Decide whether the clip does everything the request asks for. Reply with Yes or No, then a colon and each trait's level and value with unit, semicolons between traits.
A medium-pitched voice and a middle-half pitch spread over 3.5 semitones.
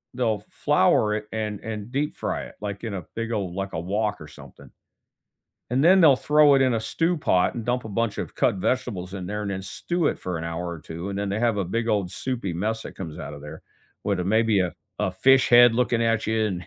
No: low, 105 Hz; average, 4.1 semitones